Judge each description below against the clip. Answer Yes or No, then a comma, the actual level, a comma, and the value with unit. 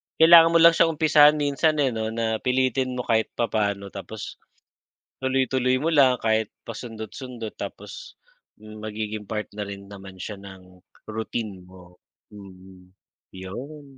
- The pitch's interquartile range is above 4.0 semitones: Yes, average, 4.7 semitones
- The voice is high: No, low, 110 Hz